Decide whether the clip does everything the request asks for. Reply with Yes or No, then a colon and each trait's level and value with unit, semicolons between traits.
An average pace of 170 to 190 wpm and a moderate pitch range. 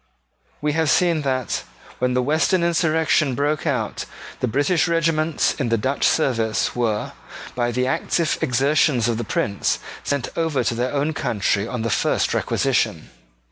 No: average, 155 wpm; average, 4.5 semitones